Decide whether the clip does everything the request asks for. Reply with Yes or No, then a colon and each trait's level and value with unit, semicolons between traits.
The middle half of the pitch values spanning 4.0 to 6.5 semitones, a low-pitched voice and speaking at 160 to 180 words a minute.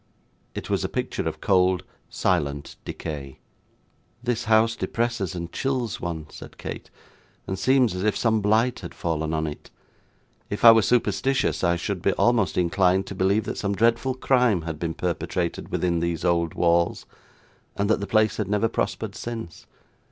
Yes: average, 4.9 semitones; low, 100 Hz; average, 165 wpm